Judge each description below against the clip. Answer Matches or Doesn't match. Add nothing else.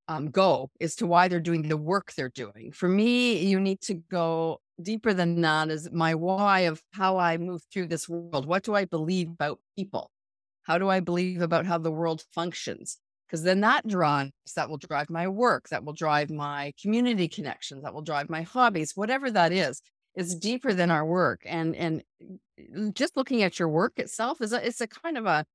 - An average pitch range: Matches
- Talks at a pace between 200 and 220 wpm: Matches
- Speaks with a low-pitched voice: Doesn't match